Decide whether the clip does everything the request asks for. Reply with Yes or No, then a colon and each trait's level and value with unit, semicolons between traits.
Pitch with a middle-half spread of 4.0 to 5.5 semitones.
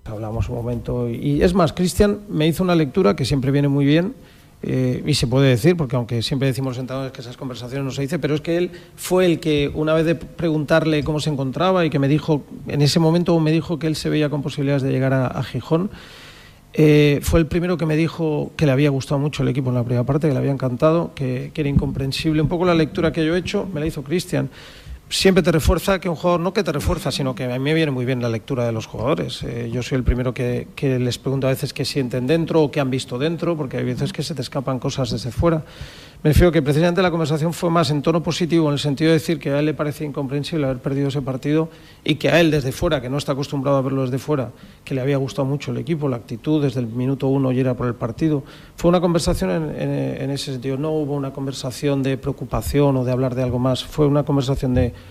No: average, 3.5 semitones